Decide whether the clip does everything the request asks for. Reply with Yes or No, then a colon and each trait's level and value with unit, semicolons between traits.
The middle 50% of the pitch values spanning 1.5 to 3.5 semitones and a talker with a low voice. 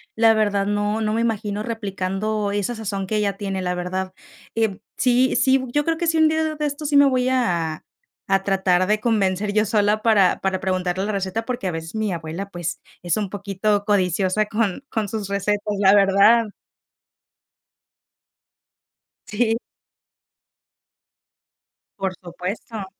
No: average, 2.8 semitones; high, 205 Hz